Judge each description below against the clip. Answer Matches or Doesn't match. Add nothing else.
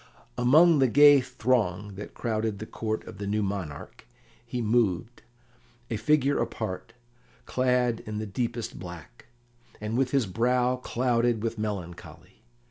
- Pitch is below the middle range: Matches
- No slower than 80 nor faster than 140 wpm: Matches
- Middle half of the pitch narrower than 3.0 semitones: Doesn't match